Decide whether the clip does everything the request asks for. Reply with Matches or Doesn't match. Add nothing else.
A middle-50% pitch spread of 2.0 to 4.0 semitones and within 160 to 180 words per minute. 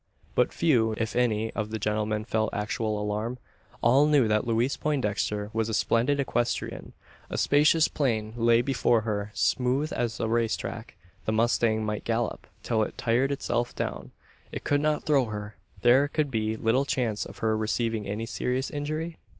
Matches